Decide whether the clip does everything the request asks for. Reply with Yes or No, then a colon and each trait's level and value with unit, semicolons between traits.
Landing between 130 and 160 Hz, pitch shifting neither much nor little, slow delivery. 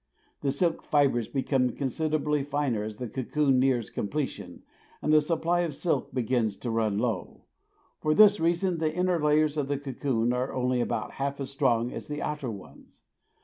No: medium, 140 Hz; average, 3.6 semitones; average, 175 wpm